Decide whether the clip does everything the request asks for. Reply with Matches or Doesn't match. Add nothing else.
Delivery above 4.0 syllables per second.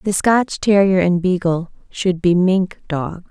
Doesn't match